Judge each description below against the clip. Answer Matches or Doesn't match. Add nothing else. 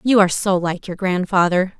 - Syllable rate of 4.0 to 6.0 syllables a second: Matches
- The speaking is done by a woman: Matches